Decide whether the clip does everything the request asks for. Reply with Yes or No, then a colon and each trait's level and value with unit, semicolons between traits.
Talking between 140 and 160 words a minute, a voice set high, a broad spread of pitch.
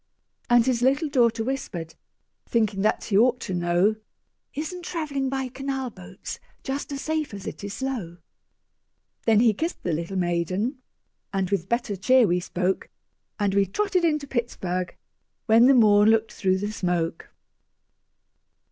Yes: average, 150 wpm; high, 220 Hz; wide, 6.0 semitones